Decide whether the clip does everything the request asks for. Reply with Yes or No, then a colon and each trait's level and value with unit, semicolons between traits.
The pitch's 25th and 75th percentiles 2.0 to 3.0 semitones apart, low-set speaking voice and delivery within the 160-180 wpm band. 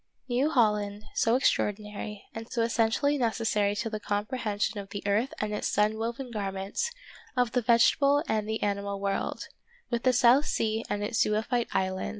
No: narrow, 2.6 semitones; high, 220 Hz; average, 165 wpm